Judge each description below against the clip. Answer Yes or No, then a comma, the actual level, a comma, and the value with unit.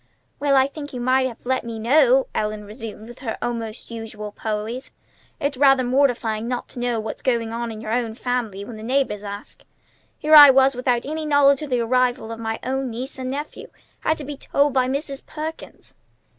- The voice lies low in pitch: No, very high, 250 Hz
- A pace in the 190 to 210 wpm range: Yes, average, 200 wpm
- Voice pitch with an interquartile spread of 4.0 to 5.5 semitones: No, average, 3.3 semitones